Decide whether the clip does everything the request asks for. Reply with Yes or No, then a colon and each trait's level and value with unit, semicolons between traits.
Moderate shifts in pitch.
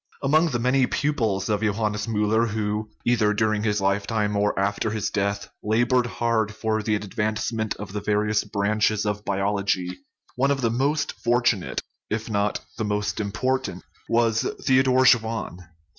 No: narrow, 2.2 semitones